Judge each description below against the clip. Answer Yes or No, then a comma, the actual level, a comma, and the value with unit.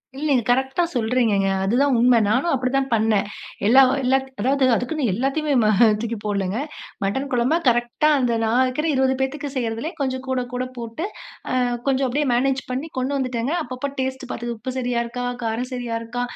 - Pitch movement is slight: Yes, narrow, 2.3 semitones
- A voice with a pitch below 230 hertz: No, very high, 255 Hz